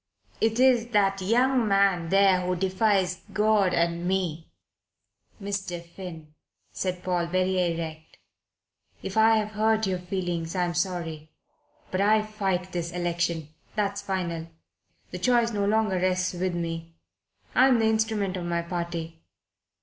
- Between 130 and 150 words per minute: Yes, average, 140 wpm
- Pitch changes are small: No, average, 3.3 semitones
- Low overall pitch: No, medium, 185 Hz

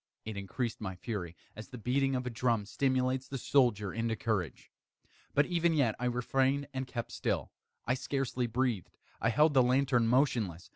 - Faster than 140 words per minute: Yes, average, 175 wpm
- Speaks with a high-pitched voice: No, low, 125 Hz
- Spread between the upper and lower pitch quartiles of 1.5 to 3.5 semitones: Yes, average, 3.1 semitones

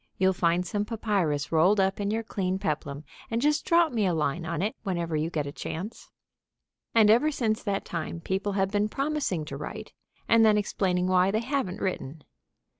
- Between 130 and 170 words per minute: No, average, 190 wpm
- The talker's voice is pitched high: Yes, high, 195 Hz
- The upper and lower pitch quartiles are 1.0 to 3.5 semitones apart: No, average, 4.5 semitones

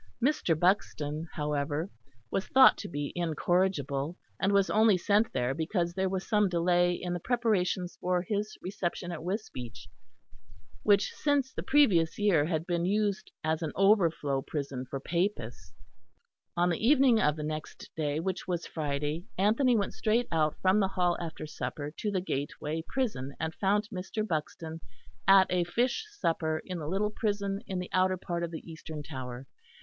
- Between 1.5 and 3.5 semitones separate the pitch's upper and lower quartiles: No, average, 4.4 semitones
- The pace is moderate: Yes, average, 165 wpm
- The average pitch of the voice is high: No, medium, 175 Hz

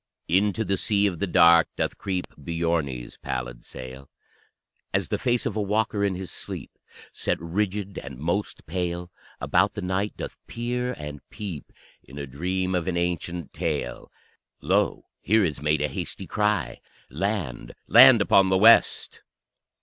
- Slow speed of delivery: No, average, 155 wpm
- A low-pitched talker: Yes, very low, 90 Hz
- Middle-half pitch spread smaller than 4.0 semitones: No, average, 4.9 semitones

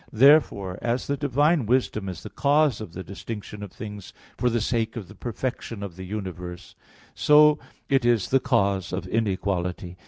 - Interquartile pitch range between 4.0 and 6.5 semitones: Yes, average, 5.2 semitones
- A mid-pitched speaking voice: No, low, 110 Hz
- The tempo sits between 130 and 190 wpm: Yes, average, 175 wpm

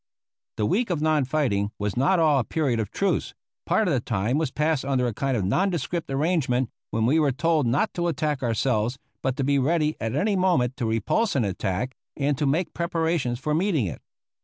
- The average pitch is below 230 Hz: Yes, medium, 140 Hz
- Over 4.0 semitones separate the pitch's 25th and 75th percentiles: Yes, average, 5.0 semitones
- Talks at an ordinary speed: No, fast, 210 wpm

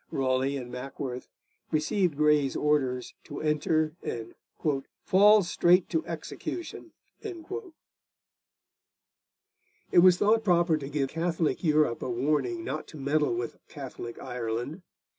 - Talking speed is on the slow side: Yes, slow, 115 wpm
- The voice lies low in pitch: No, medium, 150 Hz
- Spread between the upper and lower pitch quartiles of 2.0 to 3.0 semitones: No, average, 5.1 semitones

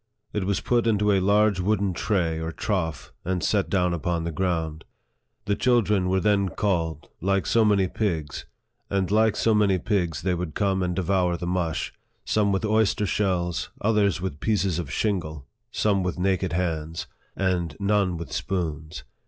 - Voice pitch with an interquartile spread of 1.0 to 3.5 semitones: Yes, average, 3.1 semitones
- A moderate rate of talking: Yes, average, 160 wpm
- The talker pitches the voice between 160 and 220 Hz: No, very low, 95 Hz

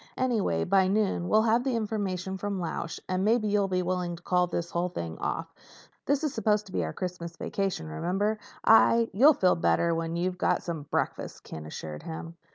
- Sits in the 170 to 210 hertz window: Yes, medium, 185 Hz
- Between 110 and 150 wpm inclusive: No, average, 195 wpm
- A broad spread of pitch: No, average, 3.9 semitones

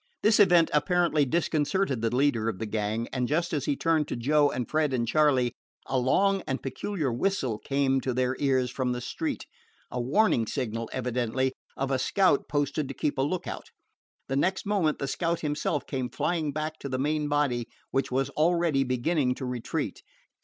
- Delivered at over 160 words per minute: Yes, average, 185 wpm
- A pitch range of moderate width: Yes, average, 3.8 semitones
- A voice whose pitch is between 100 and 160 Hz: Yes, medium, 140 Hz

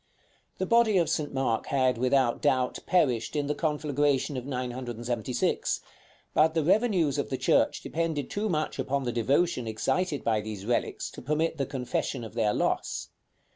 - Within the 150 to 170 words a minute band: Yes, average, 165 wpm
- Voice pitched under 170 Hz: Yes, low, 135 Hz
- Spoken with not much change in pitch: No, average, 4.4 semitones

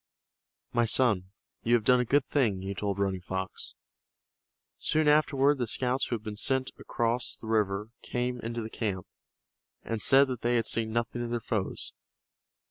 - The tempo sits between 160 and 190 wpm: Yes, average, 175 wpm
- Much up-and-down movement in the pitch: No, average, 3.1 semitones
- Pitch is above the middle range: No, low, 115 Hz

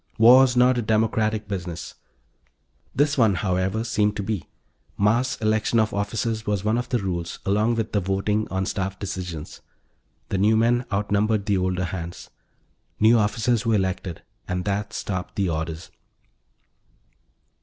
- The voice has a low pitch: Yes, low, 105 Hz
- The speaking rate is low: No, average, 150 wpm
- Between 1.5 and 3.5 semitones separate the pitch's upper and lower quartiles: Yes, average, 2.9 semitones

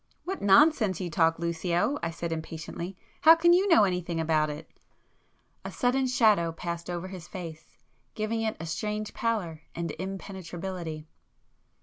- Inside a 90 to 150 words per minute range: Yes, average, 140 wpm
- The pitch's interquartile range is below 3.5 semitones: No, average, 4.6 semitones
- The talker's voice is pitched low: No, medium, 180 Hz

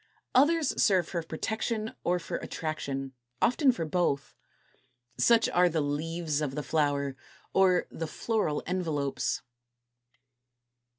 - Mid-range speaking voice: Yes, medium, 165 Hz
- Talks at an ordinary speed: No, slow, 115 wpm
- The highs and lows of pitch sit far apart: No, average, 4.8 semitones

